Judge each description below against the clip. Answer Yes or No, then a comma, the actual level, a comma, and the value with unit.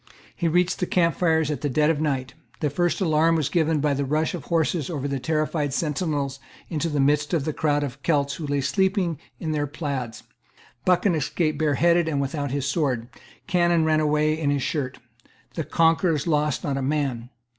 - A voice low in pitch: No, medium, 150 Hz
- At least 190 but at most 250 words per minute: Yes, average, 195 wpm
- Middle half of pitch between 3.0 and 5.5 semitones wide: No, narrow, 2.5 semitones